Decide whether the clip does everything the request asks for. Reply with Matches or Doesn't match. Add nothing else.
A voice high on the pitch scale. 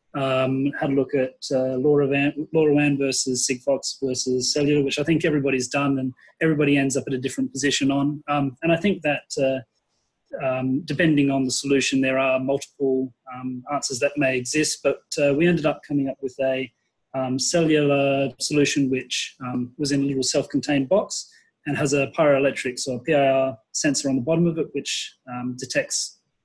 Doesn't match